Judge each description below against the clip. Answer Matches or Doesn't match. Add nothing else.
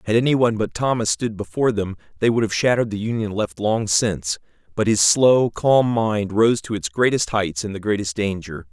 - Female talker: Doesn't match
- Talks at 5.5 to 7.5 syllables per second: Doesn't match